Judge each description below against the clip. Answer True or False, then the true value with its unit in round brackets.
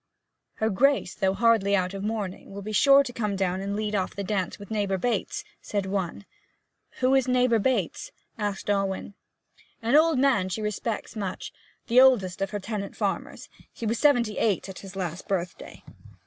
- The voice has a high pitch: True (205 Hz)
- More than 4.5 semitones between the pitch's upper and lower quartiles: False (3.4 semitones)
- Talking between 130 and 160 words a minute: False (175 wpm)